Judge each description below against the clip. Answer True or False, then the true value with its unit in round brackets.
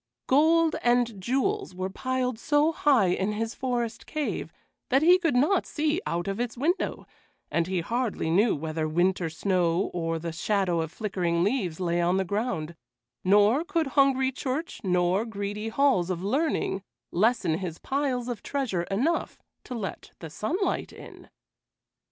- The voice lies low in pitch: False (215 Hz)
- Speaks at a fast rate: False (155 wpm)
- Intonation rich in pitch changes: True (7.1 semitones)